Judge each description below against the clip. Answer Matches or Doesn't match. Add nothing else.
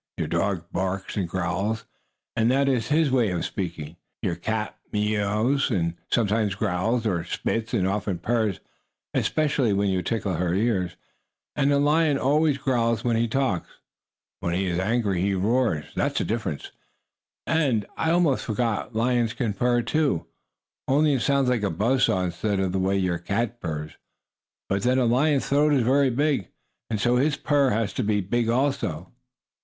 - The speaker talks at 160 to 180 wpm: Matches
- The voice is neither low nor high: Doesn't match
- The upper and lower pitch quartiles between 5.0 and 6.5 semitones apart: Matches